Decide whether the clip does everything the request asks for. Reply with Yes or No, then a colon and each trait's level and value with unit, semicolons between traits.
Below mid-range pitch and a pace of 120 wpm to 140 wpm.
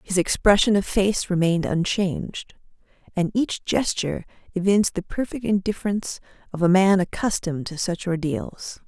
No: high, 190 Hz; slow, 135 wpm